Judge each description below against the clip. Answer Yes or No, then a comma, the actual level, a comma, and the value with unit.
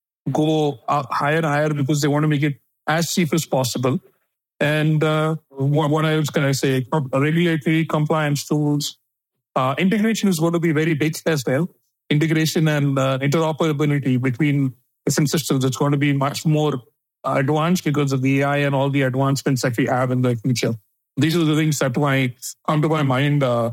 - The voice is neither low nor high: Yes, medium, 150 Hz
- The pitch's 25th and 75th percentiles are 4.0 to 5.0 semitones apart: No, narrow, 2.5 semitones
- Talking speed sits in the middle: Yes, average, 190 wpm